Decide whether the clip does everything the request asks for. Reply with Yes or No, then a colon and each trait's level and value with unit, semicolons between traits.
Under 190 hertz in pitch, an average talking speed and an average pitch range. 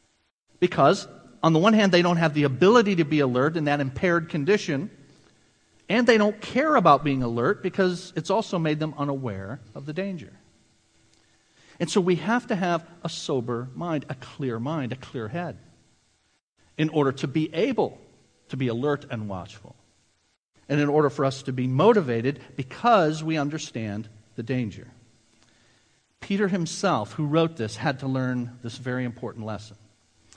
No: medium, 140 Hz; average, 165 wpm; wide, 6.2 semitones